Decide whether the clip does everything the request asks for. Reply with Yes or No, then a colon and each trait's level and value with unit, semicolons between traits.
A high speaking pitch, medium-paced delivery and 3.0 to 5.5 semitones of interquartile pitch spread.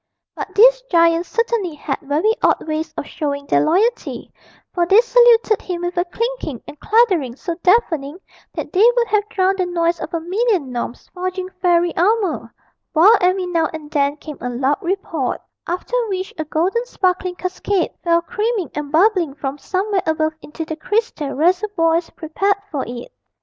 Yes: very high, 355 Hz; average, 170 wpm; average, 4.6 semitones